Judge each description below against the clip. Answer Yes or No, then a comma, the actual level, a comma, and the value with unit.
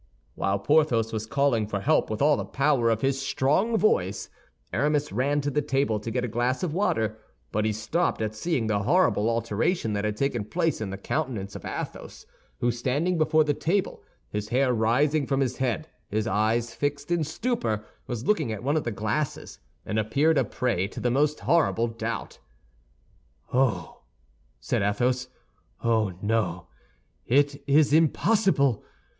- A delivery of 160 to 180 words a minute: Yes, average, 170 wpm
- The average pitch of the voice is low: Yes, low, 125 Hz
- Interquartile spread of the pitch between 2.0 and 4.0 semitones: No, average, 5.3 semitones